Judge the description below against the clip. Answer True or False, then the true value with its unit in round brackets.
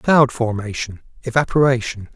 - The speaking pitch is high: False (120 Hz)